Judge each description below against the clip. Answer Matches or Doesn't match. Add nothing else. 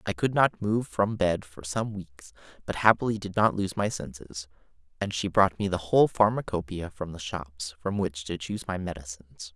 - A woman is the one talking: Doesn't match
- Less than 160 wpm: Doesn't match